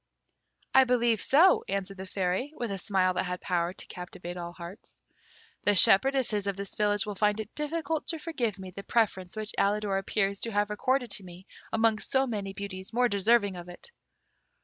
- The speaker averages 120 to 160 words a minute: No, average, 190 wpm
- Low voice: No, high, 205 Hz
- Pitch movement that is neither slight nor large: Yes, average, 3.8 semitones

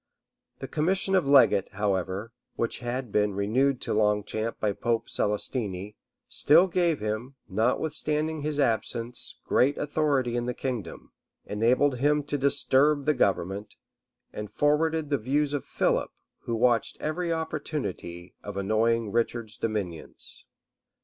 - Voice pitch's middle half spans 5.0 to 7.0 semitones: Yes, wide, 5.6 semitones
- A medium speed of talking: No, slow, 130 wpm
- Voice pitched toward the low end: Yes, low, 120 Hz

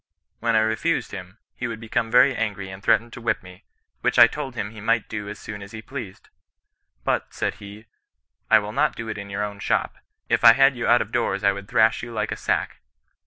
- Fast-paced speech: Yes, fast, 240 wpm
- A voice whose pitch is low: Yes, low, 110 Hz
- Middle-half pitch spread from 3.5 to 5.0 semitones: No, narrow, 2.6 semitones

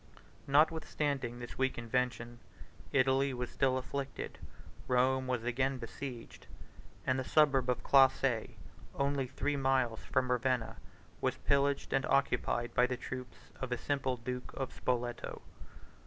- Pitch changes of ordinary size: No, narrow, 1.7 semitones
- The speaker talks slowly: Yes, slow, 130 wpm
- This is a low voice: Yes, low, 130 Hz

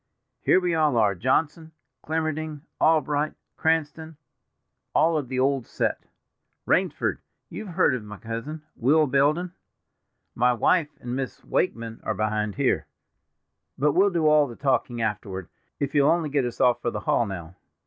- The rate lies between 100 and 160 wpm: Yes, average, 150 wpm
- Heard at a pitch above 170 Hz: No, medium, 140 Hz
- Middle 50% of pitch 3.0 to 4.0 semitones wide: No, average, 5.2 semitones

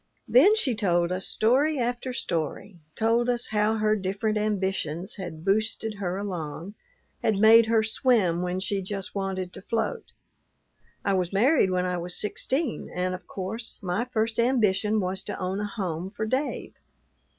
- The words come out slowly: No, average, 160 wpm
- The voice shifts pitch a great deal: No, average, 3.5 semitones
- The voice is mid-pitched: No, high, 205 Hz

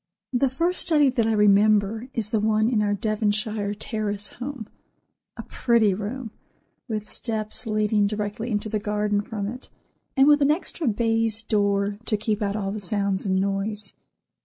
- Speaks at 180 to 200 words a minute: No, average, 160 wpm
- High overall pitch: Yes, high, 215 Hz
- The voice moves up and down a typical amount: No, narrow, 1.8 semitones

